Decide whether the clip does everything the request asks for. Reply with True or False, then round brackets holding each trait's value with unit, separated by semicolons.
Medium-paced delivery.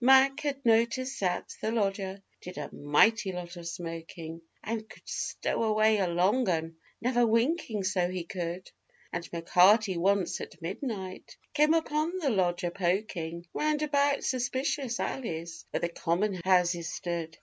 True (150 wpm)